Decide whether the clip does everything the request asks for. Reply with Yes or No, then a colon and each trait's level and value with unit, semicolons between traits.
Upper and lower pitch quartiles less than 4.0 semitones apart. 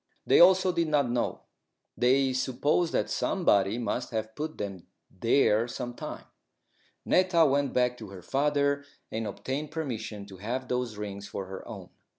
No: average, 5.1 semitones